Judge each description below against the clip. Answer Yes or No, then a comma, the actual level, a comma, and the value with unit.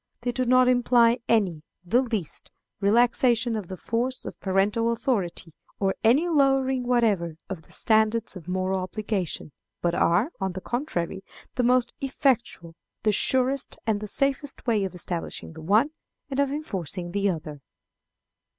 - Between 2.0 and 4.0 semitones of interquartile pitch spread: No, average, 5.1 semitones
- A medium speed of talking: Yes, average, 150 wpm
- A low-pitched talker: No, high, 220 Hz